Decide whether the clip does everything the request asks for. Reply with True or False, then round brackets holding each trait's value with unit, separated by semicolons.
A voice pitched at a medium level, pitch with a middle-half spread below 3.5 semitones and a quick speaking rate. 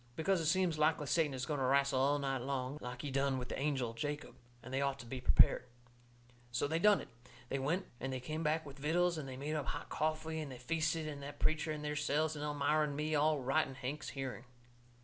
True (145 Hz; 2.6 semitones; 235 wpm)